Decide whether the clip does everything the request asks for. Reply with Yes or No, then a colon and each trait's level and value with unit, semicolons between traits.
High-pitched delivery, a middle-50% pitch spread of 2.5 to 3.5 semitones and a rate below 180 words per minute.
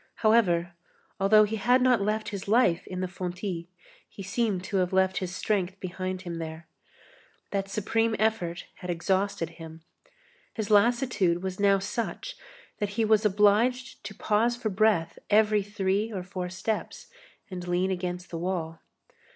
Yes: high, 195 Hz; average, 3.2 semitones; average, 155 wpm